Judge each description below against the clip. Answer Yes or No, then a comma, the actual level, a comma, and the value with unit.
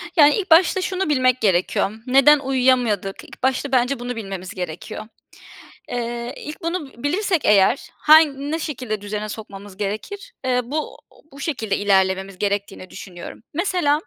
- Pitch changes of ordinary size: No, wide, 6.7 semitones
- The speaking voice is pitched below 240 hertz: No, very high, 250 Hz